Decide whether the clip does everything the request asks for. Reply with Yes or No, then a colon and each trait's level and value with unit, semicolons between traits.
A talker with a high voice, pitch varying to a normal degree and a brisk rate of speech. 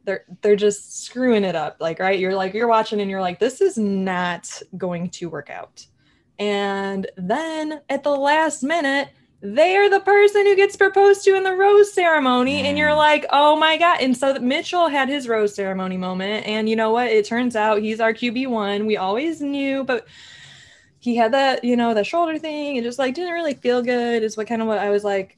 No: high, 245 Hz; wide, 6.7 semitones; fast, 215 wpm